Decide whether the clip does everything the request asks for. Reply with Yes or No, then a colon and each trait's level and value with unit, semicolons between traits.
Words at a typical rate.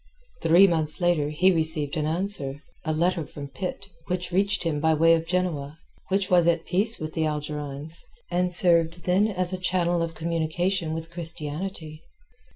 Yes: average, 160 wpm